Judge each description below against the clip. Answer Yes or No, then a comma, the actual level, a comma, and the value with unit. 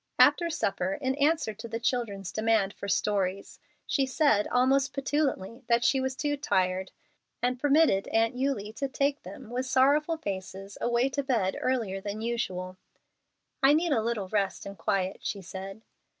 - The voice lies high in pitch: Yes, high, 230 Hz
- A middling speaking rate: Yes, average, 165 wpm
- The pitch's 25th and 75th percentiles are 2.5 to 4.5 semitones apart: No, wide, 5.5 semitones